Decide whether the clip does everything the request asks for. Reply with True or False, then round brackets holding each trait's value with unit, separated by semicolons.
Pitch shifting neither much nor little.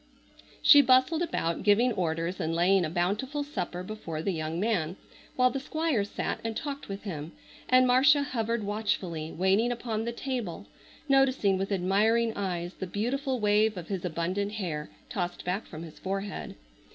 False (5.7 semitones)